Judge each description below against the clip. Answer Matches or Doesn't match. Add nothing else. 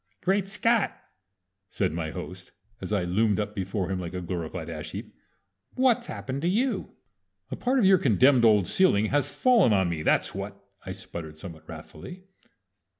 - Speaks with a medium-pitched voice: Doesn't match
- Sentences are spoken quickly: Doesn't match